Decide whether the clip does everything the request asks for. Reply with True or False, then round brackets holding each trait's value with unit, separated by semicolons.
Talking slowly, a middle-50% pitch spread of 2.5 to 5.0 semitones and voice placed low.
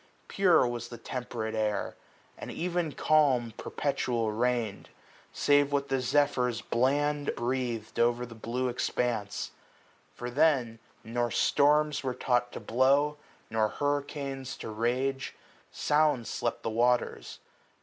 True (130 wpm; 3.3 semitones; 125 Hz)